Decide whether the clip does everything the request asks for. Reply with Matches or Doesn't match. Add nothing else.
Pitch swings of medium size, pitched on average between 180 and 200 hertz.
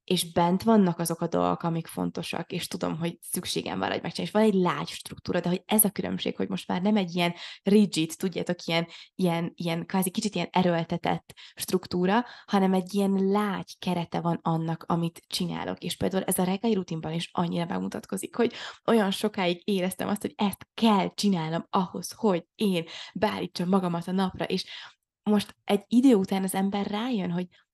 Matches